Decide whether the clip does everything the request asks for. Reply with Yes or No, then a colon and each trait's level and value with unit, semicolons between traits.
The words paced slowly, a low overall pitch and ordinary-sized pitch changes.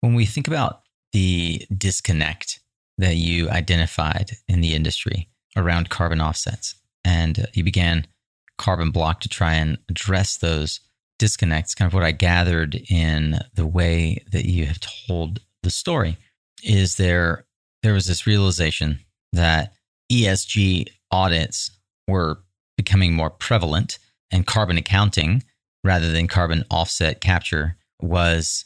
Yes: slow, 130 wpm; very low, 90 Hz; average, 3.7 semitones